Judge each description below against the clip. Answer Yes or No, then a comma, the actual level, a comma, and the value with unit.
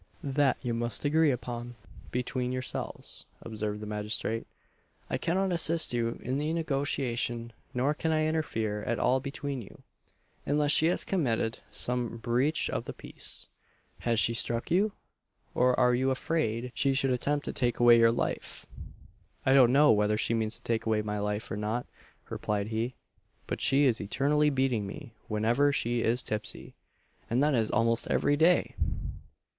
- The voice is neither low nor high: No, low, 125 Hz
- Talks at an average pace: Yes, average, 165 wpm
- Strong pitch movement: No, average, 3.9 semitones